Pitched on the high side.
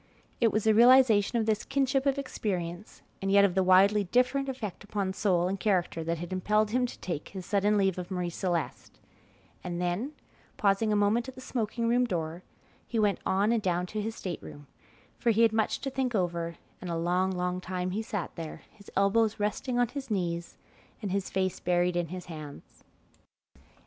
Yes: high, 200 Hz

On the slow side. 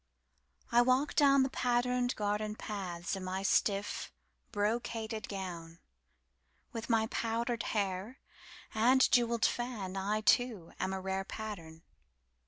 Yes: slow, 100 wpm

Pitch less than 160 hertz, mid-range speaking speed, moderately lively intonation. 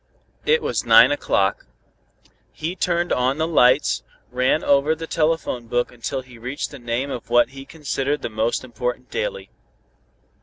Yes: low, 135 Hz; average, 155 wpm; average, 4.5 semitones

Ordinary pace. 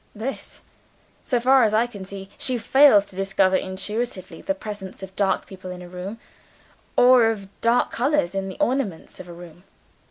Yes: average, 180 wpm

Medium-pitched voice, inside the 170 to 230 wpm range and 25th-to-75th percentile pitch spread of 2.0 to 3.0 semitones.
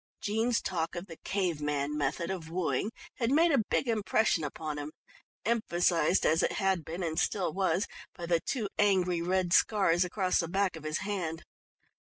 No: medium, 180 Hz; average, 180 wpm; average, 3.8 semitones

